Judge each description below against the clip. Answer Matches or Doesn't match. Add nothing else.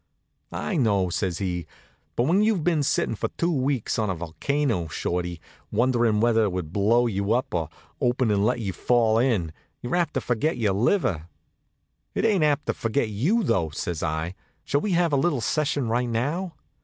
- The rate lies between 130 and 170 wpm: Doesn't match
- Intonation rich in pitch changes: Matches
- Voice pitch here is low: Matches